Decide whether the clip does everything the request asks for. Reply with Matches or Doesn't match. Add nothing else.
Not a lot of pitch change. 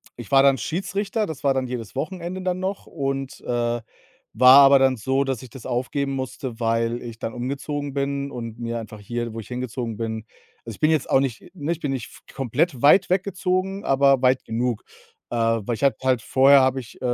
Doesn't match